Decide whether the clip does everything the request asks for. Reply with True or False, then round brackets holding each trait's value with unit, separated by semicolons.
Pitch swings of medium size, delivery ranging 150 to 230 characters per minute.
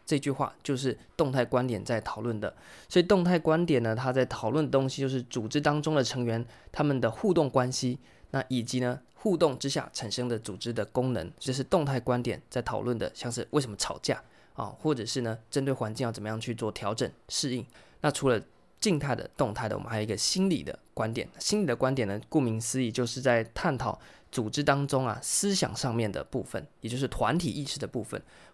False (3.7 semitones; 320 characters per minute)